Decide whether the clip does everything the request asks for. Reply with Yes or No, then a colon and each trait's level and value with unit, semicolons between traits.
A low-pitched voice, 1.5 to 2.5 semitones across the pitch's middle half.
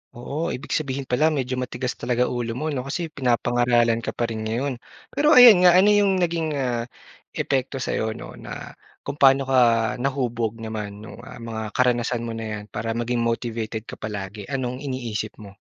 No: low, 120 Hz; average, 3.2 semitones